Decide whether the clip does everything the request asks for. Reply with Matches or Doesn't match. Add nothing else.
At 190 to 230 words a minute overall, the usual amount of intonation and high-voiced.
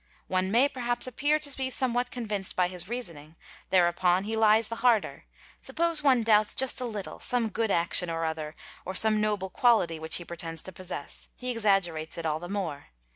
Doesn't match